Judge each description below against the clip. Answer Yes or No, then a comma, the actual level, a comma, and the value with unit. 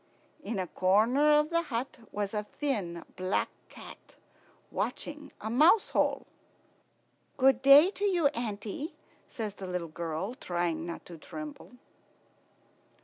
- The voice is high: Yes, high, 225 Hz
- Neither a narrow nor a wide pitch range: No, wide, 8.1 semitones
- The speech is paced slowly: Yes, slow, 130 wpm